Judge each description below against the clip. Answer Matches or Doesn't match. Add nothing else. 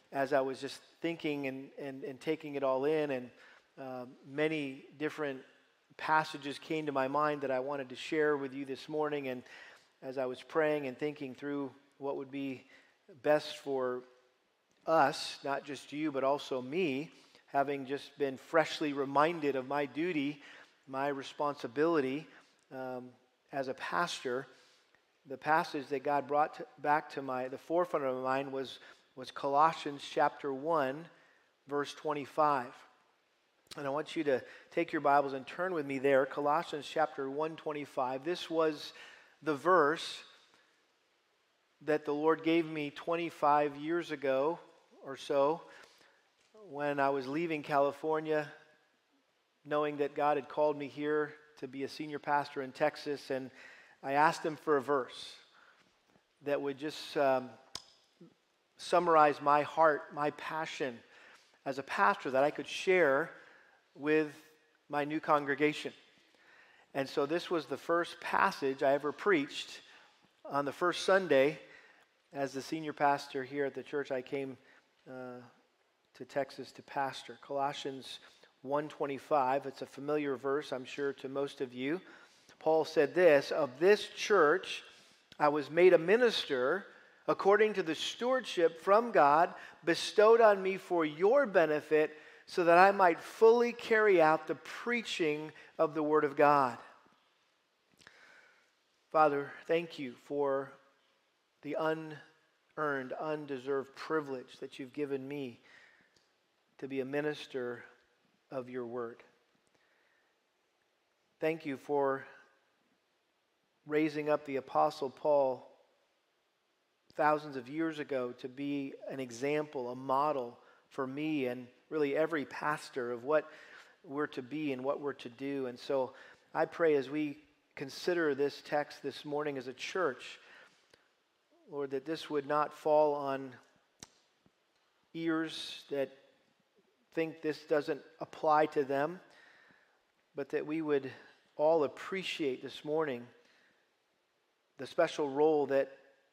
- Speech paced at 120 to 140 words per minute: Matches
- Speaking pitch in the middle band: Matches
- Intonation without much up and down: Matches